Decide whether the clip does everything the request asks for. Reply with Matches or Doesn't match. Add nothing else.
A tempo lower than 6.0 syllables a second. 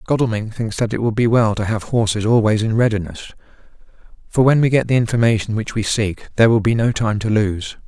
Doesn't match